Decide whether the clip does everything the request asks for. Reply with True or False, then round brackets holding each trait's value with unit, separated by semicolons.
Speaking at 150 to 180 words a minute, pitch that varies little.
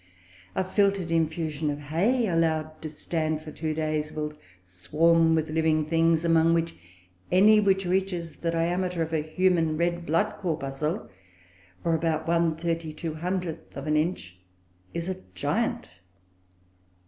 False (135 wpm; 1.8 semitones)